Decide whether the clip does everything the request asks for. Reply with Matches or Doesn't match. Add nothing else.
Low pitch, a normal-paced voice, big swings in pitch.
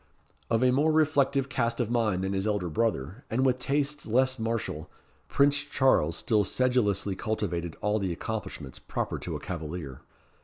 Matches